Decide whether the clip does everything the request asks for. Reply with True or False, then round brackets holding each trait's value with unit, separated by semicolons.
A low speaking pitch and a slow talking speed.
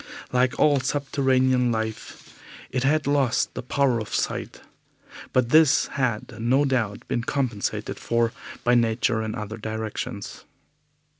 True (125 Hz; 130 wpm)